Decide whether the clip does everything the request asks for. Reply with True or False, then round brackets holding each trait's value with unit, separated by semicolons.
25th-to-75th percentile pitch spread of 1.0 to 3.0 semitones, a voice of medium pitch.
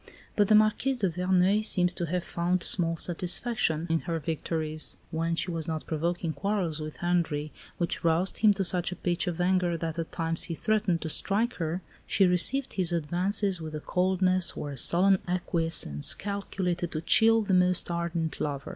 True (2.5 semitones; 175 Hz)